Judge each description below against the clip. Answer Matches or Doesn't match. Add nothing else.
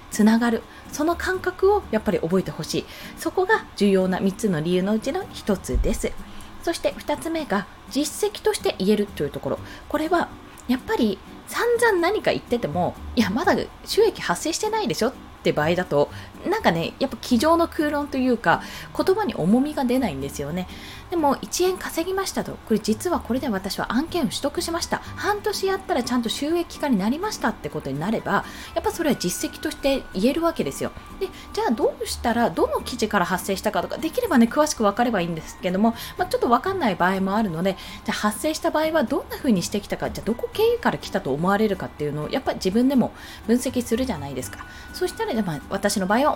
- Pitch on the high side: Matches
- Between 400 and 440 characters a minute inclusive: Matches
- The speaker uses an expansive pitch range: Matches